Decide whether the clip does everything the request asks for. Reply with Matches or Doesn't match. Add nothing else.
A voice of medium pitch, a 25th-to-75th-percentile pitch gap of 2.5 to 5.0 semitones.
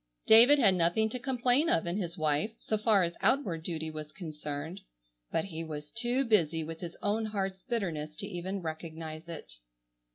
Doesn't match